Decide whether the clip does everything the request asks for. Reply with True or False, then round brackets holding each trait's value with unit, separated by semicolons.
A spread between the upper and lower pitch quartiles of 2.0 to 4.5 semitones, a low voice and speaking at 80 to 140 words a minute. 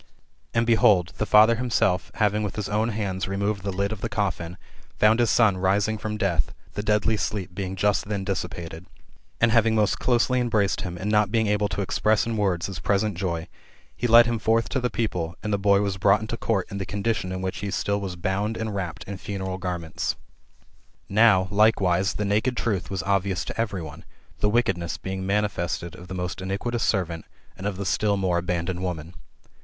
False (2.6 semitones; 100 Hz; 200 wpm)